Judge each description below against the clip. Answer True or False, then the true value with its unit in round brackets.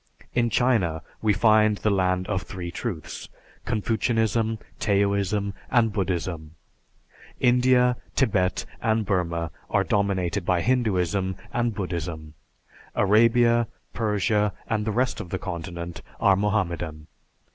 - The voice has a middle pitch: False (100 Hz)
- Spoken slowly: True (115 wpm)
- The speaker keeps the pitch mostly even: False (3.9 semitones)